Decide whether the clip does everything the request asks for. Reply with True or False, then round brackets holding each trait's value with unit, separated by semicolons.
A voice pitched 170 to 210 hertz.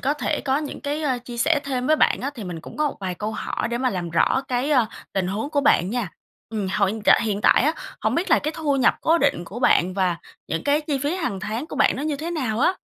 False (255 Hz)